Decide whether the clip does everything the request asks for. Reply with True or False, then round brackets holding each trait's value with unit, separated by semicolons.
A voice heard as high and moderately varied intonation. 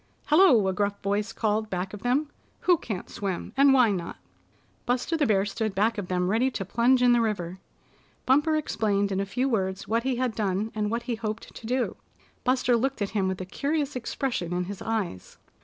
True (220 Hz; 4.4 semitones)